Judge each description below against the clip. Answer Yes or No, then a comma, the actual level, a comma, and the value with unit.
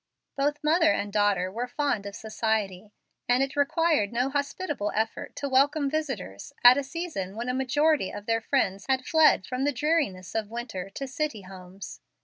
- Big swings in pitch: Yes, wide, 6.0 semitones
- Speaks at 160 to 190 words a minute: Yes, average, 175 wpm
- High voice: Yes, very high, 250 Hz